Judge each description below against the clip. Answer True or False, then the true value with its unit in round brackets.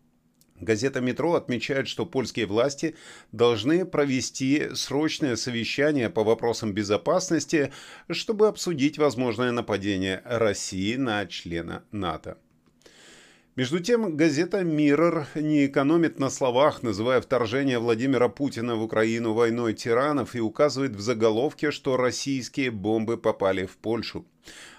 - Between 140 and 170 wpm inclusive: False (115 wpm)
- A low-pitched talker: True (125 Hz)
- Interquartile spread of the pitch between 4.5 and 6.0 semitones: True (4.9 semitones)